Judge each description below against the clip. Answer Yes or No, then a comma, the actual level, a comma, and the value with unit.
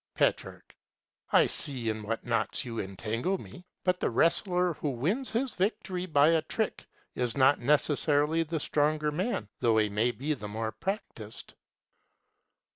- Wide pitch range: Yes, wide, 7.5 semitones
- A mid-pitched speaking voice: Yes, medium, 145 Hz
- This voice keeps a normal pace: Yes, average, 150 wpm